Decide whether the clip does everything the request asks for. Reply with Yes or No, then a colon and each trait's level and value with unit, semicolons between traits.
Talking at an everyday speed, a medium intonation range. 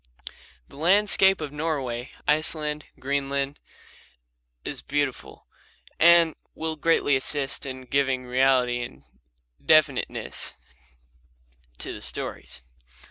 No: slow, 95 wpm; average, 3.1 semitones